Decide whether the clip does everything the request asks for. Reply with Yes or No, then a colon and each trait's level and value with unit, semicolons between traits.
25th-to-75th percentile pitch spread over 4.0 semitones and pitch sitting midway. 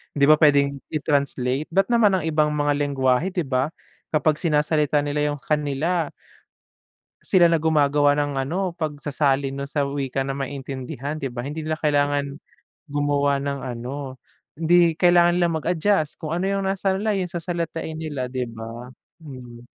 No: average, 2.9 semitones; medium, 145 Hz